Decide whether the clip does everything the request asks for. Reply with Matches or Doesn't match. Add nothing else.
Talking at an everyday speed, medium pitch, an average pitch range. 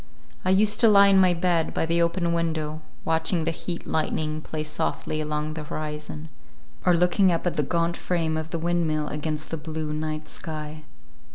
Doesn't match